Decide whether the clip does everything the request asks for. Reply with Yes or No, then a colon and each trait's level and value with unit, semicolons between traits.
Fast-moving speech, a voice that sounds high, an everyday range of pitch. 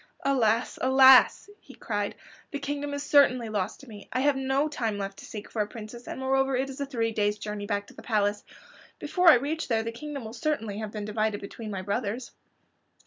Yes: fast, 215 wpm; high, 235 Hz; average, 4.5 semitones